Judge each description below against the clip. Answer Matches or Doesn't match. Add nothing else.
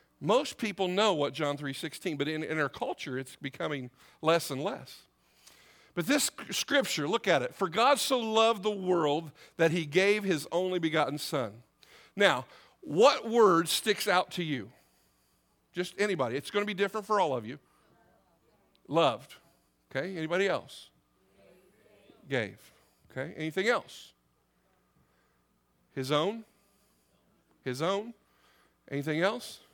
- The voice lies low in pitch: Doesn't match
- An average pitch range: Doesn't match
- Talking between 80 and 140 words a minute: Matches